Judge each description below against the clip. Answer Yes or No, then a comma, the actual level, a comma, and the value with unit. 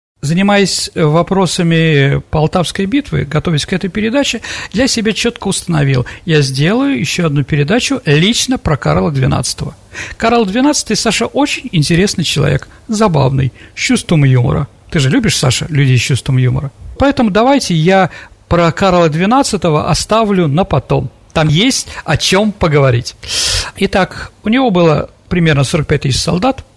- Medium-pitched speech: Yes, medium, 170 Hz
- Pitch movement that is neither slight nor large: No, wide, 7.0 semitones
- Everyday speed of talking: Yes, average, 135 wpm